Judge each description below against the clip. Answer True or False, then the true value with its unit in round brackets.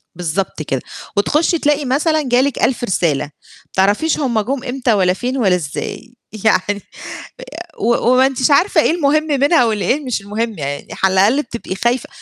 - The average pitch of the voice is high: True (240 Hz)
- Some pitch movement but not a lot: False (6.4 semitones)